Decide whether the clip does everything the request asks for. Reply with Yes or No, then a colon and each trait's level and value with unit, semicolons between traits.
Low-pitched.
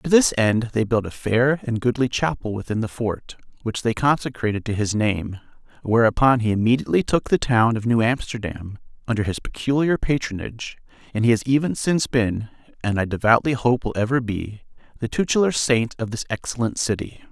Yes: low, 120 Hz